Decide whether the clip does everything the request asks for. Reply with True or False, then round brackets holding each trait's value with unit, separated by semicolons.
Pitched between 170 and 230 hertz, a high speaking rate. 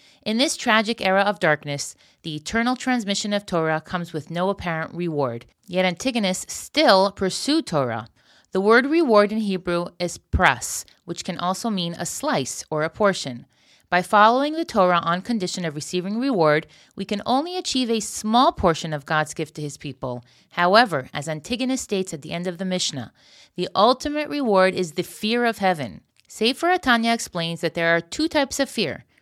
False (190 Hz; 180 wpm)